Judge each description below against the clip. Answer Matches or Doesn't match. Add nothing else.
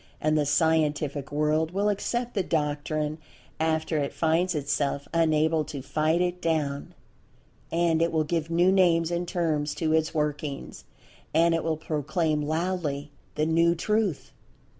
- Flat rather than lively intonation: Matches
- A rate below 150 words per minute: Matches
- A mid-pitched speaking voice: Matches